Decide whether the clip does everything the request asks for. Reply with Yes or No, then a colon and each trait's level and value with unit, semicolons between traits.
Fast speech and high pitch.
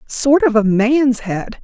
No: average, 185 wpm; high, 245 Hz